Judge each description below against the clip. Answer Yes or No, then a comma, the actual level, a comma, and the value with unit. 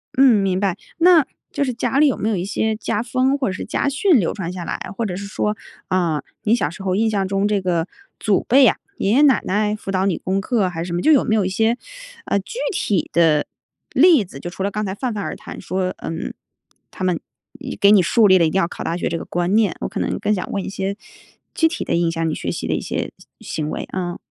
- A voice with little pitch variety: No, average, 4.0 semitones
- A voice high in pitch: Yes, high, 195 Hz